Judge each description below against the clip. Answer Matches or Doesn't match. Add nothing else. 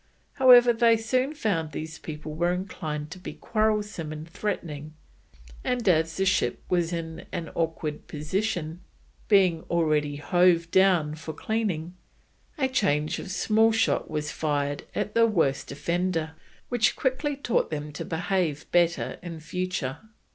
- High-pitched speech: Doesn't match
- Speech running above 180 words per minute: Doesn't match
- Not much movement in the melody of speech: Doesn't match